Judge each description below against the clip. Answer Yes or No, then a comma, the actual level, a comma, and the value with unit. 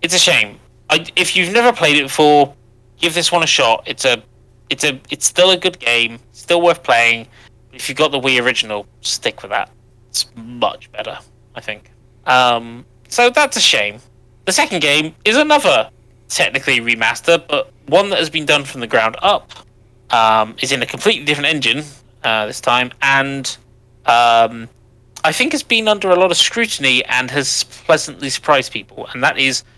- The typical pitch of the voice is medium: No, low, 130 Hz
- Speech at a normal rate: Yes, average, 185 wpm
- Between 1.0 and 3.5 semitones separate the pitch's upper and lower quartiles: No, average, 5.1 semitones